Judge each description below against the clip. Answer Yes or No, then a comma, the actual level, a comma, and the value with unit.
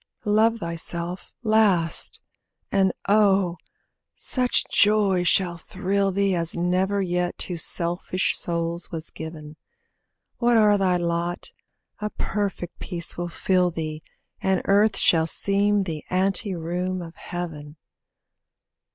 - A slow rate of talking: Yes, slow, 115 wpm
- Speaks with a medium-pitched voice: Yes, medium, 180 Hz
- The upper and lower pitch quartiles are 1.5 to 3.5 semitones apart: Yes, average, 2.7 semitones